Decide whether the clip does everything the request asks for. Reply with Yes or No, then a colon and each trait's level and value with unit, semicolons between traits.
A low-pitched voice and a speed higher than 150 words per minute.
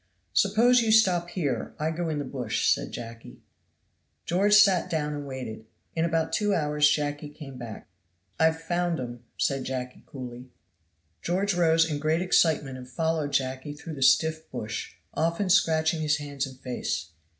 No: medium, 150 Hz; average, 160 wpm